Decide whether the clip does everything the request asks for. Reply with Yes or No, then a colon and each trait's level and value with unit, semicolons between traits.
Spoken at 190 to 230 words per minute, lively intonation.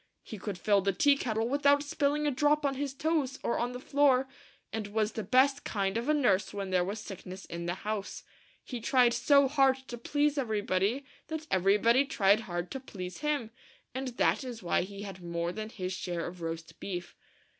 Yes: fast, 205 wpm; wide, 6.2 semitones